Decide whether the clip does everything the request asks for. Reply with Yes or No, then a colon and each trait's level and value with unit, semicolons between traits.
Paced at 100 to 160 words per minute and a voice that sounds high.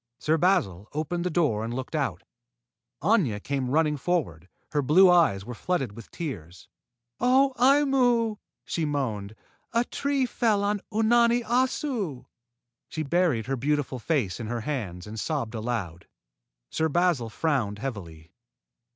No: average, 140 wpm; medium, 150 Hz